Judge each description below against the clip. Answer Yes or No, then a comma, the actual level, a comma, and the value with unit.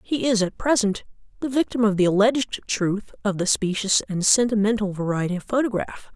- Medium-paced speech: Yes, average, 175 wpm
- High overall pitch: Yes, high, 210 Hz